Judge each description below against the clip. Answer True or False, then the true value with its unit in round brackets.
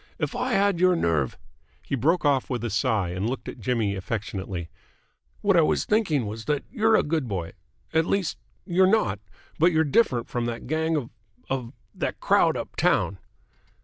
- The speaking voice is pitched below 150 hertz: True (135 Hz)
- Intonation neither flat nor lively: False (7.8 semitones)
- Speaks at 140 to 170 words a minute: False (185 wpm)